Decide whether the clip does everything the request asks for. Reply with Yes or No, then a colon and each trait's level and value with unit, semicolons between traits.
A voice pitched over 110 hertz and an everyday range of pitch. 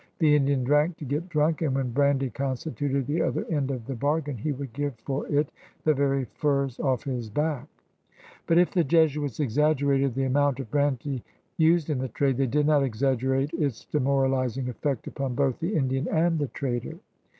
No: medium, 140 Hz; narrow, 2.2 semitones